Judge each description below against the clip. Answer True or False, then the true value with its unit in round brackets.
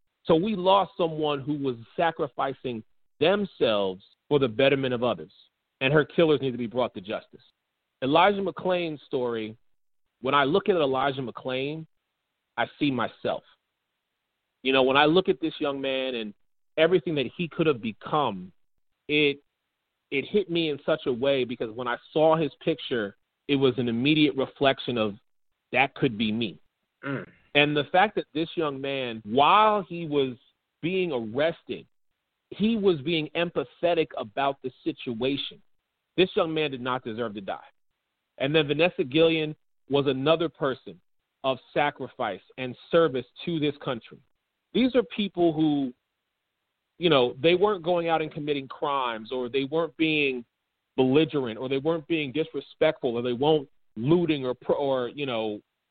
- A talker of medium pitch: True (145 Hz)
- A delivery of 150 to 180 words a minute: True (160 wpm)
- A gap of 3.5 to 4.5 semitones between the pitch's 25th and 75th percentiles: True (4.2 semitones)